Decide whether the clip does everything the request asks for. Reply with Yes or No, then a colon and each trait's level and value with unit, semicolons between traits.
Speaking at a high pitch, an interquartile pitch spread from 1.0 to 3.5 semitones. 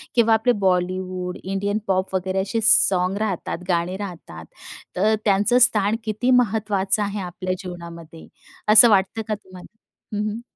Yes: high, 195 Hz; average, 2.8 semitones